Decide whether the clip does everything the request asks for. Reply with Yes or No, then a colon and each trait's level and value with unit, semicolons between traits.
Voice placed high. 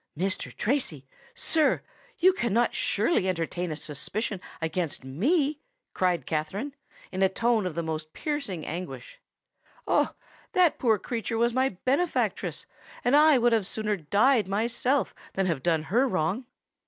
Yes: high, 210 Hz